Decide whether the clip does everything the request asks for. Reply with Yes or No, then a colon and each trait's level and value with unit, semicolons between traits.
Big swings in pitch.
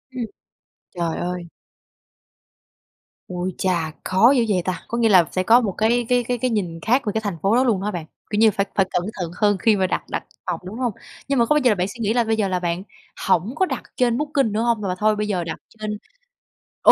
No: average, 4.2 semitones